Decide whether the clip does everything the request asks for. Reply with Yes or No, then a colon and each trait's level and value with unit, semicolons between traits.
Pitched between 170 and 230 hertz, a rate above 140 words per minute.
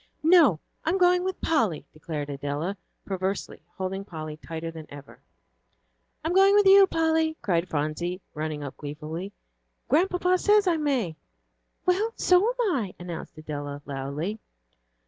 No: high, 190 Hz; slow, 135 wpm